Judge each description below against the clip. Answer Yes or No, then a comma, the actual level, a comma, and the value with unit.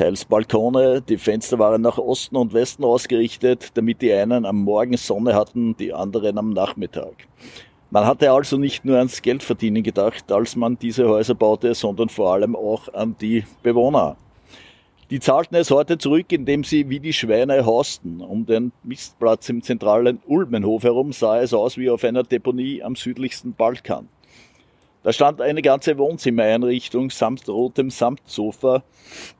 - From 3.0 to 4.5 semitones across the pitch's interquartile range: No, narrow, 2.6 semitones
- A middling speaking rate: Yes, average, 155 wpm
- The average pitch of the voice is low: Yes, low, 120 Hz